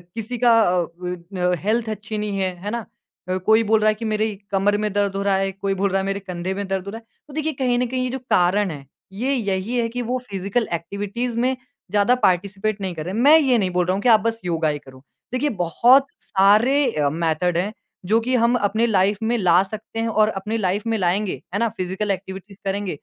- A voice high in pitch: Yes, high, 205 Hz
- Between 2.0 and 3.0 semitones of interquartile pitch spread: No, average, 3.4 semitones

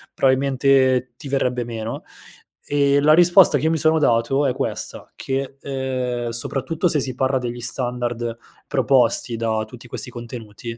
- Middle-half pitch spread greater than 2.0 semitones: Yes, narrow, 2.6 semitones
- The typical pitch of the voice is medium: No, low, 130 Hz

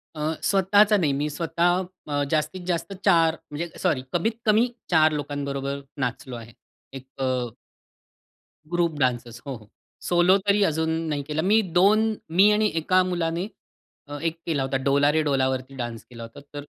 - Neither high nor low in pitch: Yes, medium, 155 Hz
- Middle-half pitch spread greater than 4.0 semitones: Yes, average, 4.9 semitones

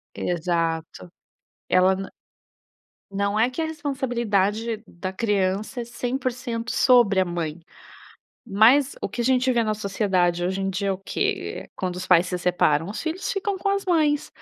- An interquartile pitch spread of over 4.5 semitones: Yes, wide, 5.5 semitones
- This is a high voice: Yes, high, 210 Hz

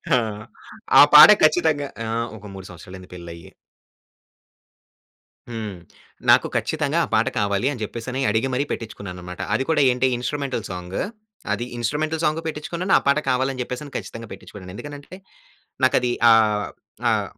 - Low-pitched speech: Yes, low, 125 Hz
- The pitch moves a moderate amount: No, wide, 6.0 semitones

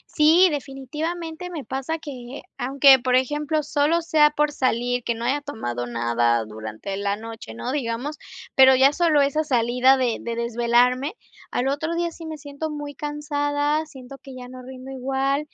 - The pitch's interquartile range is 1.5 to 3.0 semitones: No, average, 3.6 semitones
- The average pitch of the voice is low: No, very high, 270 Hz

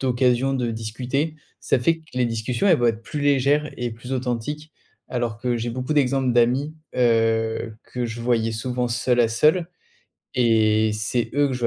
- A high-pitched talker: No, low, 125 Hz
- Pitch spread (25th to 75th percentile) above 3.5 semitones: No, average, 2.9 semitones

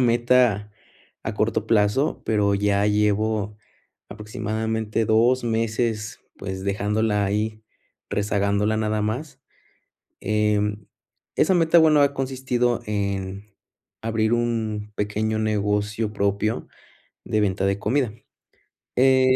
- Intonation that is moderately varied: No, narrow, 2.1 semitones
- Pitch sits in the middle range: No, low, 110 Hz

